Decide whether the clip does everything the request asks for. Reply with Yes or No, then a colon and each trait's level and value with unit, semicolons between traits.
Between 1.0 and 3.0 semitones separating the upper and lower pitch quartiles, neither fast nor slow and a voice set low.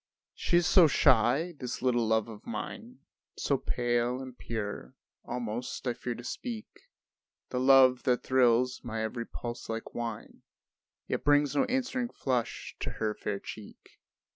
Yes: average, 2.7 semitones; average, 150 wpm; low, 125 Hz